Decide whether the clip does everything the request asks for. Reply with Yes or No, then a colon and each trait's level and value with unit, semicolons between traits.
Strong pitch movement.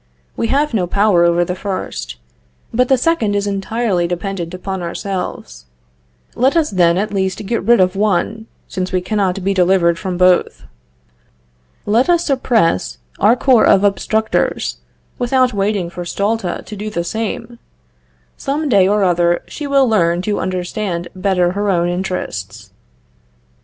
No: average, 3.8 semitones